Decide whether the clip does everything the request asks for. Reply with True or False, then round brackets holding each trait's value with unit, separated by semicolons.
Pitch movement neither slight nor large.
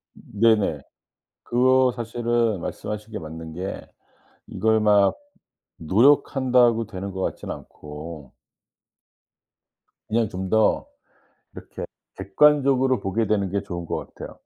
True (4.2 semitones)